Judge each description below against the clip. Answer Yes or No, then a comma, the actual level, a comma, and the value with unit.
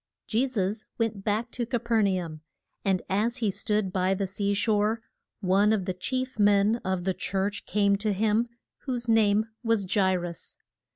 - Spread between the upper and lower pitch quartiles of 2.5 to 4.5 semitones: Yes, average, 2.8 semitones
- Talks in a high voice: Yes, high, 205 Hz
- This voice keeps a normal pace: Yes, average, 185 wpm